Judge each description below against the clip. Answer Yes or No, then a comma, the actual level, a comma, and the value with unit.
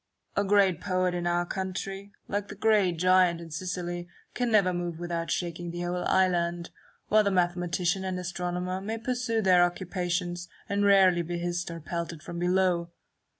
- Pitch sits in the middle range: Yes, medium, 180 Hz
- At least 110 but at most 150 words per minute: No, average, 165 wpm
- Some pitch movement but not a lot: No, narrow, 1.7 semitones